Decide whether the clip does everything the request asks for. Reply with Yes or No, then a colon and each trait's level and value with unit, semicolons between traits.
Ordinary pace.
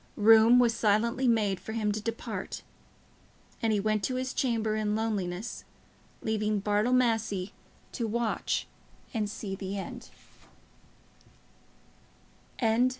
No: slow, 115 wpm